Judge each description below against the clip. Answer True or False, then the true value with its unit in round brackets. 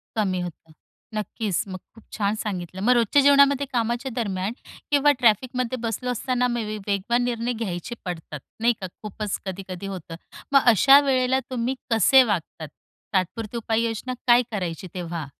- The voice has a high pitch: True (225 Hz)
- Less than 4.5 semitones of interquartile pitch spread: False (4.8 semitones)